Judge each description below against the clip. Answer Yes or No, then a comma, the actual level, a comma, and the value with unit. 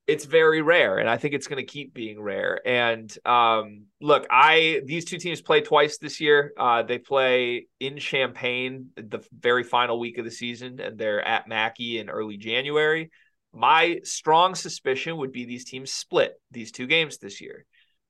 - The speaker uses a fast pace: No, average, 180 wpm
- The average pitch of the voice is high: No, low, 130 Hz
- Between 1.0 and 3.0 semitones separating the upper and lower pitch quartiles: No, average, 4.6 semitones